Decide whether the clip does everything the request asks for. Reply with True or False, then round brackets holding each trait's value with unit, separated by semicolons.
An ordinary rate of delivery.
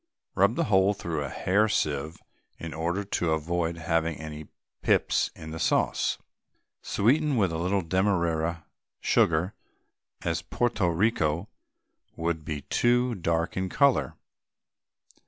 False (125 wpm)